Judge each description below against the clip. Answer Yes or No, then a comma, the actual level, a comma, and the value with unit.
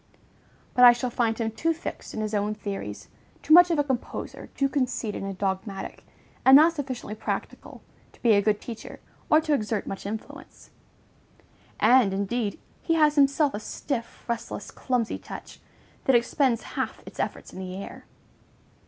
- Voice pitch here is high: Yes, high, 235 Hz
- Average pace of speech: Yes, average, 165 wpm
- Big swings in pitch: No, average, 4.8 semitones